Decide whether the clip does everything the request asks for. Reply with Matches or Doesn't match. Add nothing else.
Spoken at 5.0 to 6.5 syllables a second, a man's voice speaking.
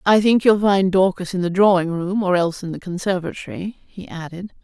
Doesn't match